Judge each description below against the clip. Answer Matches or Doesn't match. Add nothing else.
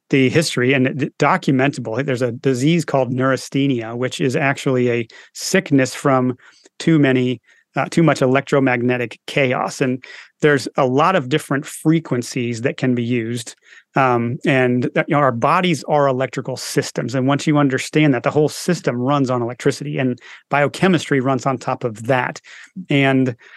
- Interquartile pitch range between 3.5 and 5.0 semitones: Doesn't match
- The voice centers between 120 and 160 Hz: Matches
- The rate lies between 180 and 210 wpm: Doesn't match